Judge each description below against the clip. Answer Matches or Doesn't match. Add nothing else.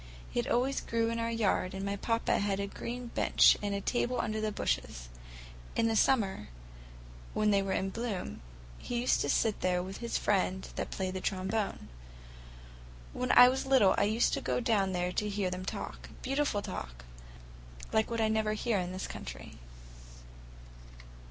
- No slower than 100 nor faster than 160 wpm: Doesn't match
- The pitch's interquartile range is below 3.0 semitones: Doesn't match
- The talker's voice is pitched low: Doesn't match